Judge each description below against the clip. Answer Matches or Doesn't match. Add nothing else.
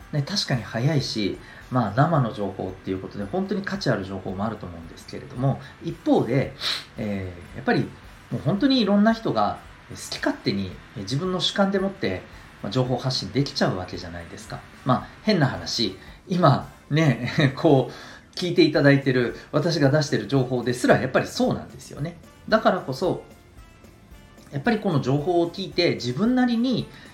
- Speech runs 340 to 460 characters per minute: Matches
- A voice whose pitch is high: Doesn't match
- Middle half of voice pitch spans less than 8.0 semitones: Doesn't match